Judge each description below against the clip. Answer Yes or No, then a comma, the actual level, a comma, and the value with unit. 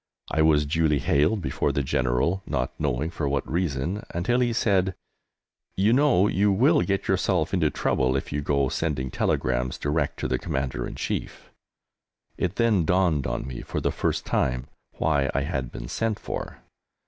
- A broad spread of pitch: Yes, wide, 5.8 semitones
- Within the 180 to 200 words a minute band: No, average, 170 wpm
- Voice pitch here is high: No, very low, 80 Hz